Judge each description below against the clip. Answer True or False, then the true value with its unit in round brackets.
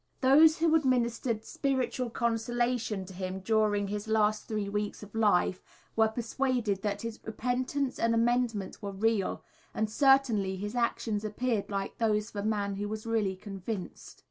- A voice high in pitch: True (220 Hz)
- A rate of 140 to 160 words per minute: True (155 wpm)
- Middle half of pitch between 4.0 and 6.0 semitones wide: False (2.9 semitones)